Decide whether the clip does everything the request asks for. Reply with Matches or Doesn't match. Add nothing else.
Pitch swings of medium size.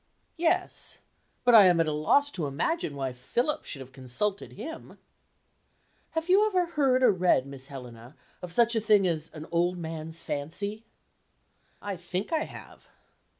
Doesn't match